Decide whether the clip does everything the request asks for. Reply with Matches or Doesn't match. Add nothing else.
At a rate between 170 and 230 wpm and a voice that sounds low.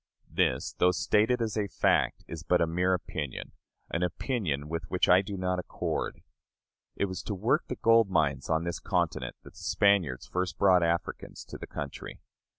Matches